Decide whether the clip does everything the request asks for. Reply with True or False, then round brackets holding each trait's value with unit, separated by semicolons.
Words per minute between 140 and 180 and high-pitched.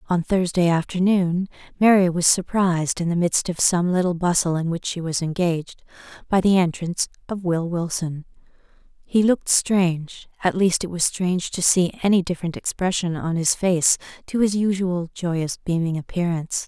False (165 wpm; 175 Hz)